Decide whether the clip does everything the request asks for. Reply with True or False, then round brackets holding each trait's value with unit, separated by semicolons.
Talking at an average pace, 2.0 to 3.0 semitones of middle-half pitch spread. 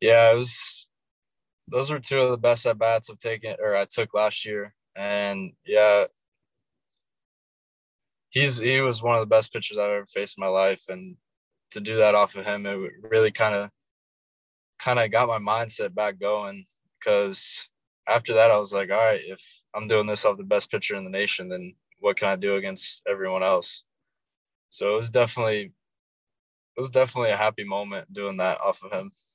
True (190 wpm; 2.5 semitones)